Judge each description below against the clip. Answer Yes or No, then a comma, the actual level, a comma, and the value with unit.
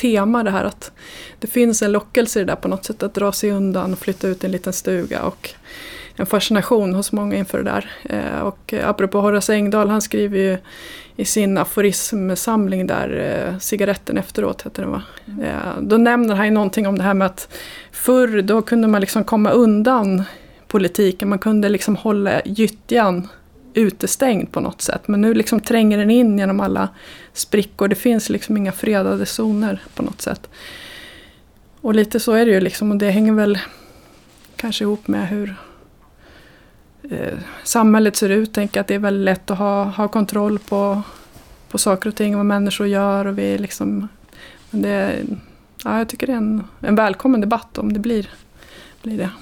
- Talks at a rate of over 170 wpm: Yes, average, 185 wpm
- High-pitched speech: Yes, high, 205 Hz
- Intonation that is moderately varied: No, narrow, 1.9 semitones